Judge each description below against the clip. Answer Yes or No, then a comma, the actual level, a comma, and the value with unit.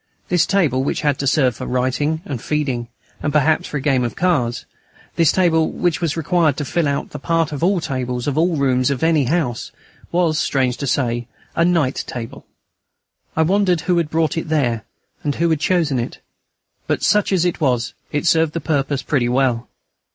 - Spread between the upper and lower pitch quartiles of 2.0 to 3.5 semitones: No, average, 4.3 semitones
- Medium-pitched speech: Yes, medium, 150 Hz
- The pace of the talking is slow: No, average, 200 wpm